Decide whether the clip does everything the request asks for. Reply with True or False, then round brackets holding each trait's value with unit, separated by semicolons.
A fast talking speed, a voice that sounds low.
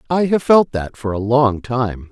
True (225 wpm; 125 Hz)